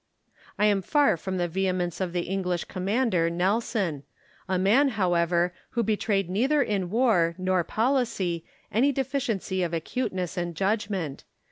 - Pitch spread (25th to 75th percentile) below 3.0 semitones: No, average, 4.1 semitones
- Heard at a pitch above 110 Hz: Yes, high, 190 Hz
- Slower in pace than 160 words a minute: Yes, average, 145 wpm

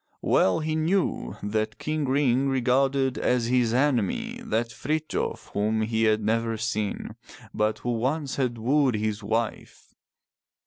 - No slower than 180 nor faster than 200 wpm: No, slow, 135 wpm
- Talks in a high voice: No, low, 120 Hz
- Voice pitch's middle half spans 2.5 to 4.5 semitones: Yes, average, 3.9 semitones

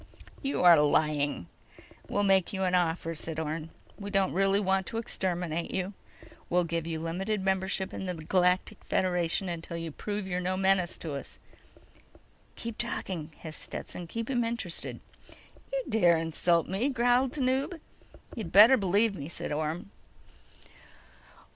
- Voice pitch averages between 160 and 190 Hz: Yes, medium, 185 Hz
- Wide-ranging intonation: No, average, 3.6 semitones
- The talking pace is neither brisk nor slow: Yes, average, 150 wpm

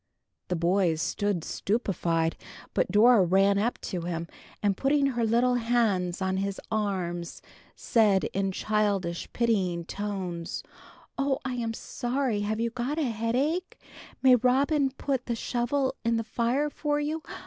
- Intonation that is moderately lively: Yes, average, 4.8 semitones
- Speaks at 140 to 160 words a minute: Yes, average, 150 wpm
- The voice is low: No, high, 220 Hz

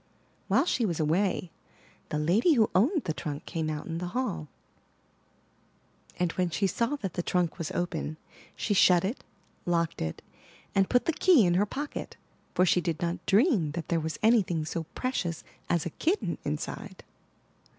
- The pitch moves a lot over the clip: No, average, 4.9 semitones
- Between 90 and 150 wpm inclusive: No, average, 170 wpm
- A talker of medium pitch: Yes, medium, 175 Hz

